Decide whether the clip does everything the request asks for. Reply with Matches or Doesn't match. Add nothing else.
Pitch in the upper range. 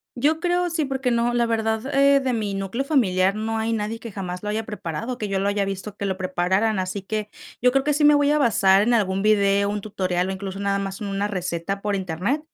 Matches